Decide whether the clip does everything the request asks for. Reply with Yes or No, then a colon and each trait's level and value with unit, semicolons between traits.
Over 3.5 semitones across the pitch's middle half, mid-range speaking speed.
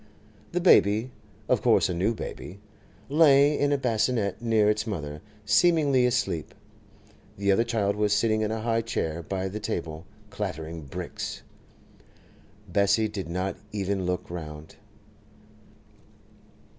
No: average, 4.0 semitones; slow, 120 wpm